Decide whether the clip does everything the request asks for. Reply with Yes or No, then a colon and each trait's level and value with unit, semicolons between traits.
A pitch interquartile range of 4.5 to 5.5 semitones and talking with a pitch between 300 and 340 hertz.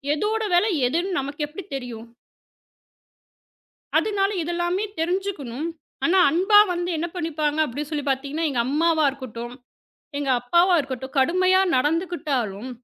Yes: average, 4.8 semitones; very high, 310 Hz